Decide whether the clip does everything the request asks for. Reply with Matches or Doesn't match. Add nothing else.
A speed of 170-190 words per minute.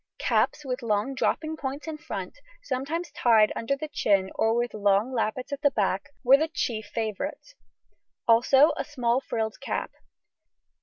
Doesn't match